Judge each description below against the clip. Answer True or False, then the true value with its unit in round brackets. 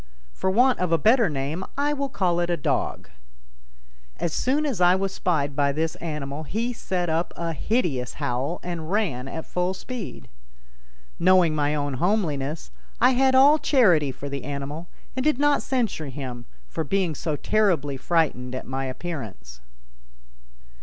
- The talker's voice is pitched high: False (170 Hz)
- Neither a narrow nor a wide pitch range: False (6.9 semitones)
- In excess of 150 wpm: True (160 wpm)